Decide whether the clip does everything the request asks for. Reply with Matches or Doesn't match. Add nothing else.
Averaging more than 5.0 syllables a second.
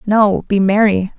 Doesn't match